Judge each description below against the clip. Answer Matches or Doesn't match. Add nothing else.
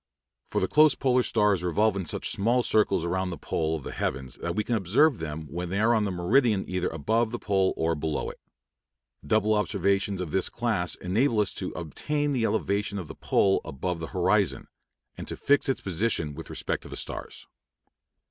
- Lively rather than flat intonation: Doesn't match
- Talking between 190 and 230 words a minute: Matches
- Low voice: Matches